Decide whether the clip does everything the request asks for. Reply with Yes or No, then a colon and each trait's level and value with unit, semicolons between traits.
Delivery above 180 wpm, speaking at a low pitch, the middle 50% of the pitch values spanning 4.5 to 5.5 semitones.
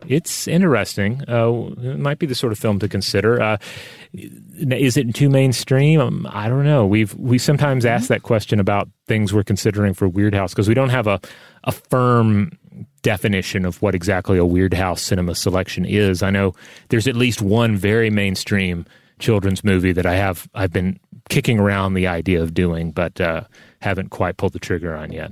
Yes: average, 190 wpm; low, 105 Hz; average, 4.8 semitones